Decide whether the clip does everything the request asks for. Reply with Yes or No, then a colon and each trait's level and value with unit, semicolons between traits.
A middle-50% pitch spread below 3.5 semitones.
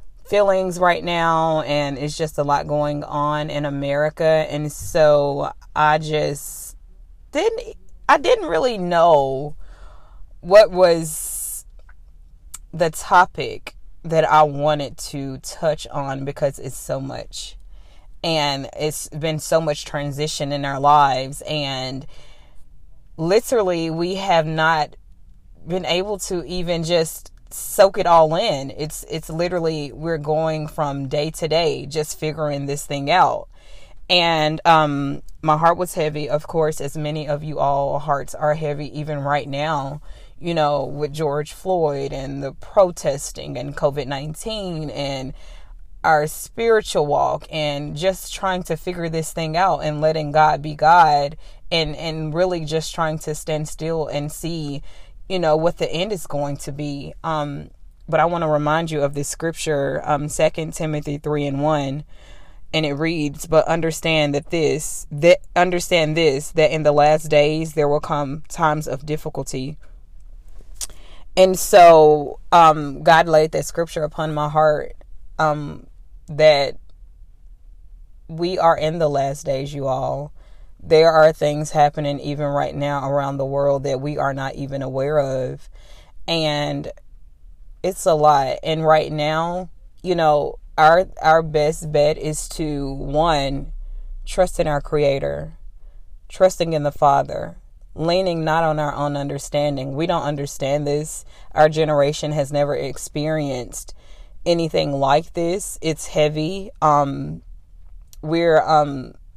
Yes: narrow, 2.4 semitones